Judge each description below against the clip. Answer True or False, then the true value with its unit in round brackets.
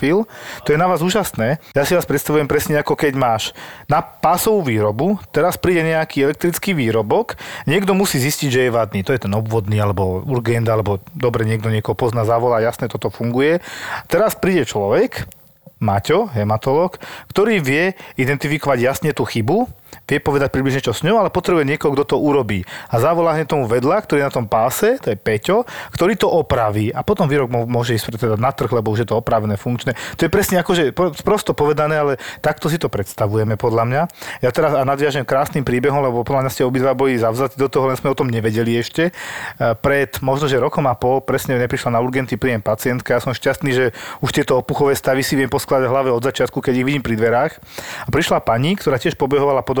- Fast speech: True (200 wpm)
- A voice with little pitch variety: False (4.1 semitones)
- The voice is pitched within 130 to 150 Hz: True (135 Hz)